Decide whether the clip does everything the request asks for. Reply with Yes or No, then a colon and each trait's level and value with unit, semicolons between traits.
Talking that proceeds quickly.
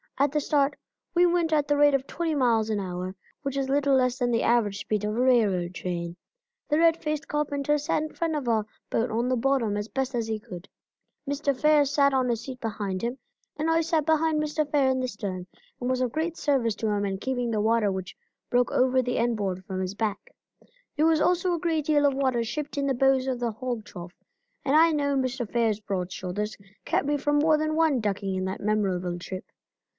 Yes: fast, 230 wpm